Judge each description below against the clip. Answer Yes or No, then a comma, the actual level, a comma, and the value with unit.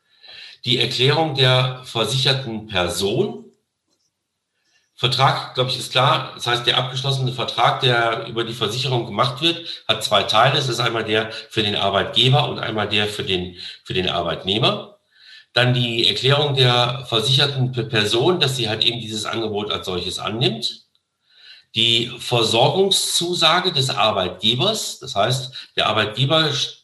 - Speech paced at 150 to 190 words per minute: No, average, 140 wpm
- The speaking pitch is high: No, low, 125 Hz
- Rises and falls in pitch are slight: No, average, 3.2 semitones